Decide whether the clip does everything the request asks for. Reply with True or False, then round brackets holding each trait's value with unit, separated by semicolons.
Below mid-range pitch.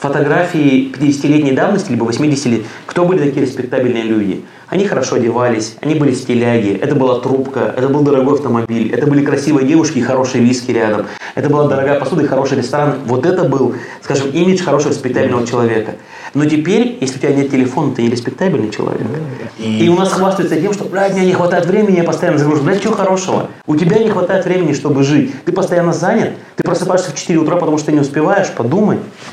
False (145 Hz)